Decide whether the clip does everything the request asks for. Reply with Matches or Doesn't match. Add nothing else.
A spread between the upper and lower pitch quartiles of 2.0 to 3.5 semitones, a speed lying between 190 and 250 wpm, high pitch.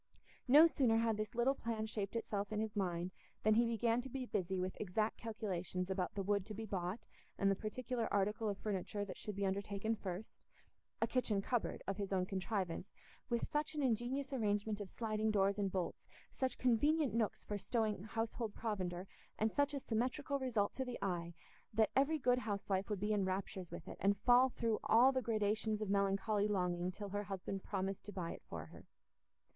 Matches